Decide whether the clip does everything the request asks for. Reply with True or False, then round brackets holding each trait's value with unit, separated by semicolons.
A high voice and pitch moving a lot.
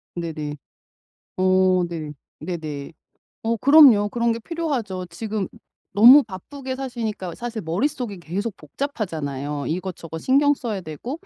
True (200 Hz; 6.3 semitones)